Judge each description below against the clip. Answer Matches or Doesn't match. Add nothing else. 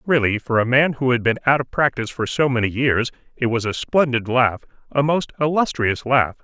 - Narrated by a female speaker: Doesn't match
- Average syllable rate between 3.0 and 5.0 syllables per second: Doesn't match